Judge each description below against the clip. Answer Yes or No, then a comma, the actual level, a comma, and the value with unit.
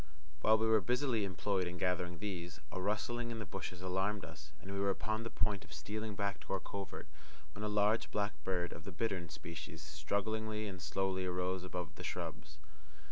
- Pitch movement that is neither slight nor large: Yes, average, 3.3 semitones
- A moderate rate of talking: Yes, average, 195 wpm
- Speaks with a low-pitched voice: Yes, very low, 95 Hz